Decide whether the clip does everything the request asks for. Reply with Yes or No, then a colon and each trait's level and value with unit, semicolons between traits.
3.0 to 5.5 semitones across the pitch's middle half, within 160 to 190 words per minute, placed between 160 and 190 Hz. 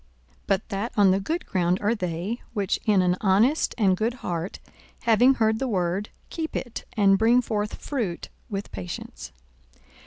No: average, 3.8 semitones; average, 165 wpm; high, 205 Hz